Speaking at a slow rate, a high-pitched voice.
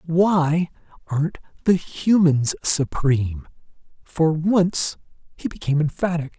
No: slow, 95 wpm; medium, 160 Hz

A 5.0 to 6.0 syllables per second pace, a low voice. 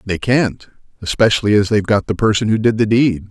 Yes: 5.9 syllables/s; low, 105 Hz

